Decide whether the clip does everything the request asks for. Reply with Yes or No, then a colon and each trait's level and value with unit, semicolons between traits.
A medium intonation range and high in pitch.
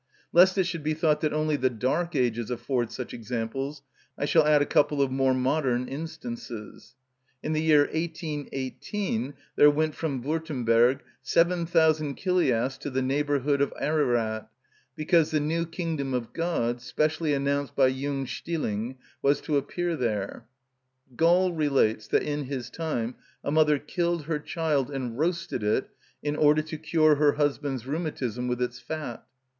No: average, 3.6 semitones; medium, 145 Hz